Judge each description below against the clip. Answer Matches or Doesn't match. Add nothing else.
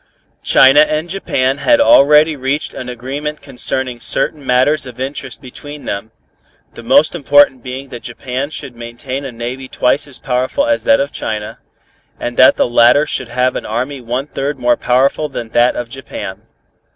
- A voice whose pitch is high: Doesn't match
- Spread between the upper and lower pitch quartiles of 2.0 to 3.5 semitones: Matches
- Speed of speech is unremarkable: Matches